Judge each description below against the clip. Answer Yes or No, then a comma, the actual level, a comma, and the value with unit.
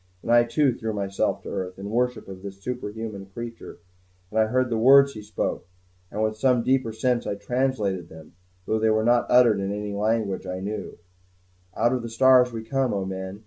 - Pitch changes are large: No, average, 3.6 semitones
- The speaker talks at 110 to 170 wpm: No, fast, 205 wpm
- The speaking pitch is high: No, low, 110 Hz